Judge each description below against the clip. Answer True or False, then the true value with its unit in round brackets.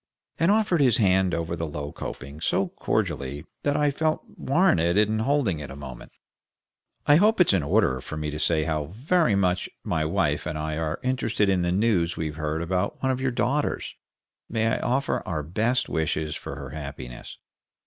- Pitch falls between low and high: False (90 Hz)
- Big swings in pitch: True (8.6 semitones)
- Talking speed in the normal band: True (190 wpm)